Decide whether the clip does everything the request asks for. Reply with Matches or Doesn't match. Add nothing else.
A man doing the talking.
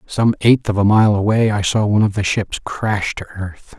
Matches